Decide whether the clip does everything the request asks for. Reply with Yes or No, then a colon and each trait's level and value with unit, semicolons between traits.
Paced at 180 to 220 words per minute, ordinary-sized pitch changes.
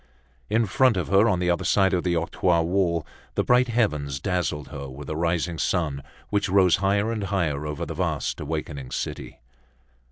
Yes: average, 185 wpm; average, 4.3 semitones